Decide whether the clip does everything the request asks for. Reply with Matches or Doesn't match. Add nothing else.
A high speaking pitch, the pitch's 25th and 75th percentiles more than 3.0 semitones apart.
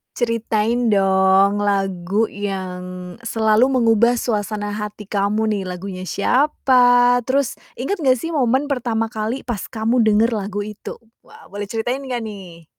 Matches